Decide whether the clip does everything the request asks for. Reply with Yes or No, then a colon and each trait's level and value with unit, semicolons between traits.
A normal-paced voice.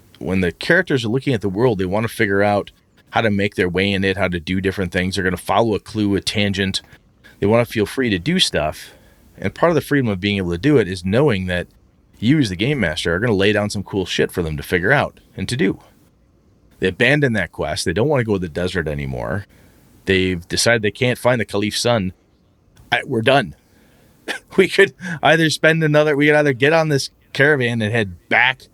No: fast, 240 wpm